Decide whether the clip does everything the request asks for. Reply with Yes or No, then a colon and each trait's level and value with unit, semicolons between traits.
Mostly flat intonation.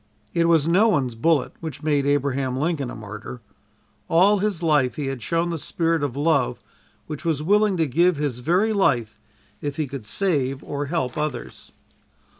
No: average, 3.9 semitones